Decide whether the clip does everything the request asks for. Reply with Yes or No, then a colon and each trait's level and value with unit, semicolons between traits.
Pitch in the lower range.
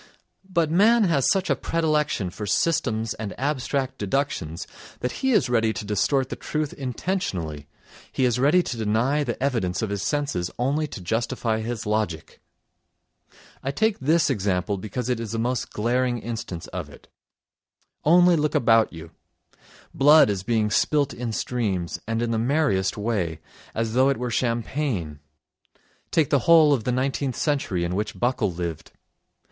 Yes: low, 120 Hz